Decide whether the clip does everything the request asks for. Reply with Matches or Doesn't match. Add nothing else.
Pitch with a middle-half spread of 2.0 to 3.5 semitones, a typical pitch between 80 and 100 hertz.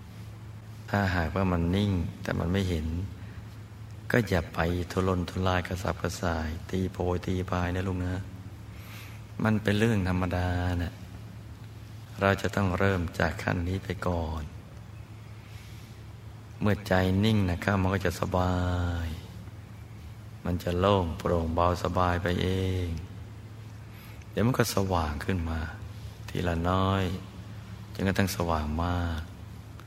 Matches